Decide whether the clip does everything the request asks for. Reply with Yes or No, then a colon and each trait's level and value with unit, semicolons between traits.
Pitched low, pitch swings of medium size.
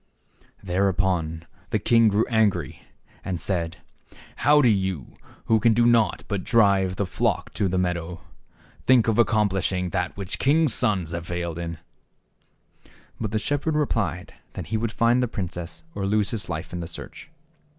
Yes: low, 100 Hz; average, 4.3 semitones